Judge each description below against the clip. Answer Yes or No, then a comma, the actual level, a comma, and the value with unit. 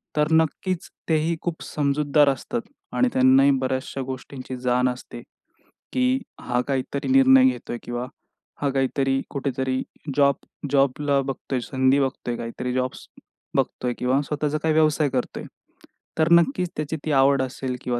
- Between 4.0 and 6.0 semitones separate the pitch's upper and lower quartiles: No, average, 2.9 semitones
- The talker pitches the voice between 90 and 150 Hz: Yes, medium, 140 Hz